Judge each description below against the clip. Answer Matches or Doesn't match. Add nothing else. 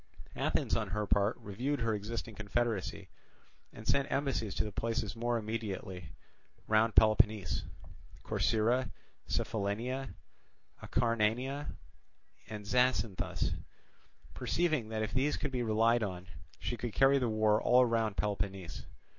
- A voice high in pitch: Doesn't match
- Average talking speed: Doesn't match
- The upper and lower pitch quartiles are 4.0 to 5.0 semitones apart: Doesn't match